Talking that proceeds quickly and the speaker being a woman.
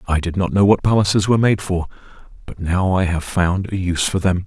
No: fast, 240 wpm; male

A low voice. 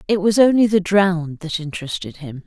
No: medium, 180 Hz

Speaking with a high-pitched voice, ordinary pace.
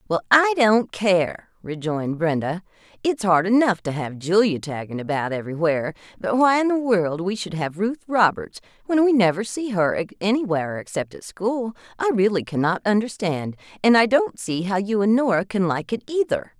Yes: high, 195 Hz; average, 180 wpm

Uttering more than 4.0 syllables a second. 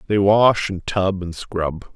No: 3.5 syllables/s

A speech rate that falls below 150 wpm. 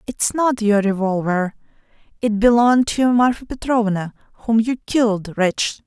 Yes: slow, 135 wpm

